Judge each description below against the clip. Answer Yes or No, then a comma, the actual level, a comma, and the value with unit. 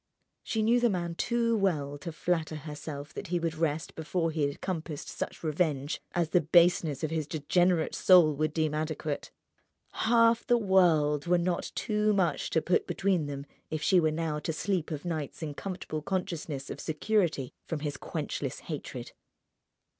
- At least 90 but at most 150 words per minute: No, average, 170 wpm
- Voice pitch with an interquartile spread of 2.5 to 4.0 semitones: Yes, average, 3.2 semitones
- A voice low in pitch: No, medium, 165 Hz